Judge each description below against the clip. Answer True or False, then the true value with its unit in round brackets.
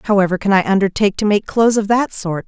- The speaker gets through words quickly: True (240 wpm)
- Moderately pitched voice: False (200 Hz)